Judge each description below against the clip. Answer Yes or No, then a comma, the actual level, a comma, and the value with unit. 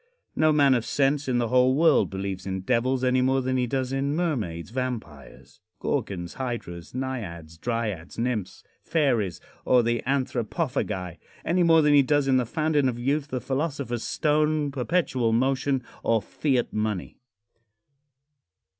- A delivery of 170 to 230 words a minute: No, average, 145 wpm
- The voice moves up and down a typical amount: Yes, average, 3.8 semitones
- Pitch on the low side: Yes, low, 130 Hz